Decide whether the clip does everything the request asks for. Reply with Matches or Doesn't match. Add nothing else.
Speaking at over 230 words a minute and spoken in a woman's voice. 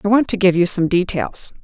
Matches